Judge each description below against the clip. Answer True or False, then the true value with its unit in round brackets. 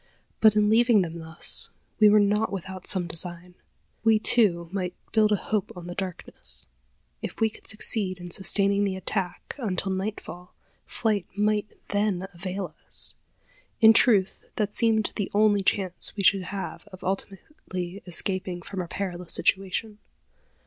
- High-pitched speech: True (195 Hz)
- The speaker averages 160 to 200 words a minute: False (150 wpm)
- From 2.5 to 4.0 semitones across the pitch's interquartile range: True (2.8 semitones)